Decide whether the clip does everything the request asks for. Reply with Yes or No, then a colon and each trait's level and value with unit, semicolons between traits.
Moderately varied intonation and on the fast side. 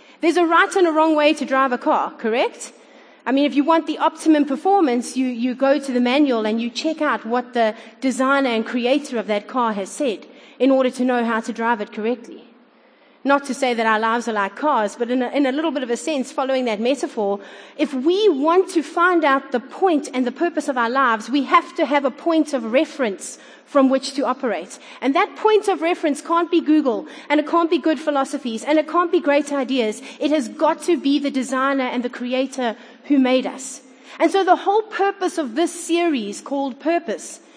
Yes: average, 4.3 semitones; fast, 225 wpm